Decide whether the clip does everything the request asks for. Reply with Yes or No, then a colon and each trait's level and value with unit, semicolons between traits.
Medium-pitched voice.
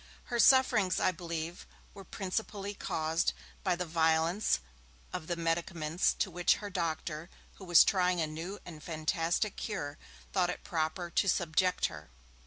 Yes: medium, 175 Hz